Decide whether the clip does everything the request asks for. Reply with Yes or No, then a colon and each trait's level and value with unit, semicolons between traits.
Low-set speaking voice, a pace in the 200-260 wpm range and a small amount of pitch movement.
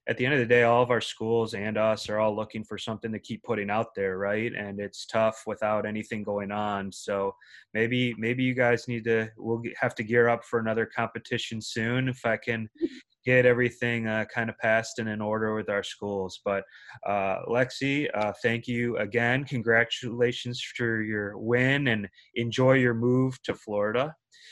No: low, 115 Hz; average, 190 wpm; narrow, 2.1 semitones